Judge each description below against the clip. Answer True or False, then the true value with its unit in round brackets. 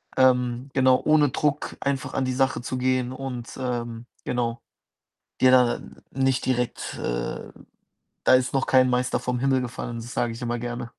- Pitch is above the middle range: False (125 Hz)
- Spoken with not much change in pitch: True (1.4 semitones)